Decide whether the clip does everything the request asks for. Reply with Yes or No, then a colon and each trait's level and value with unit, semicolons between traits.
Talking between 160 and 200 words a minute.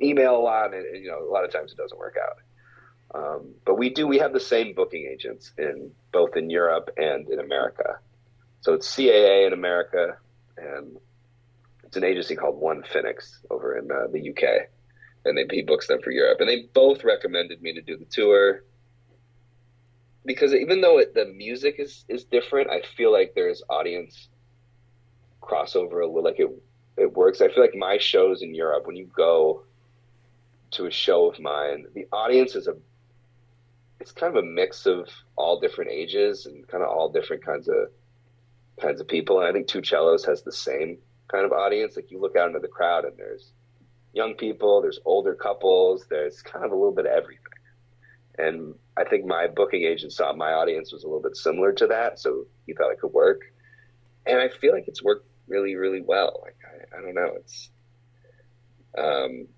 Yes: average, 195 wpm